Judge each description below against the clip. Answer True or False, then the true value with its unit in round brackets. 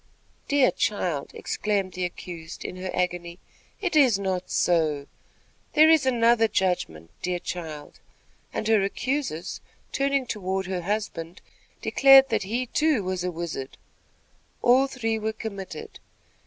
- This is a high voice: True (195 Hz)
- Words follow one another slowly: True (130 wpm)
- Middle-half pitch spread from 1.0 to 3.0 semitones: False (5.5 semitones)